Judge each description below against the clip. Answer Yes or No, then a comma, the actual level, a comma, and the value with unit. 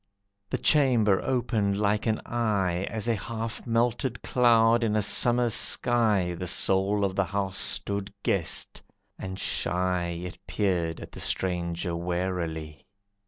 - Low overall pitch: Yes, low, 100 Hz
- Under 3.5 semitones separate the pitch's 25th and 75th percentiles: No, average, 4.0 semitones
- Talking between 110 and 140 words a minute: Yes, slow, 135 wpm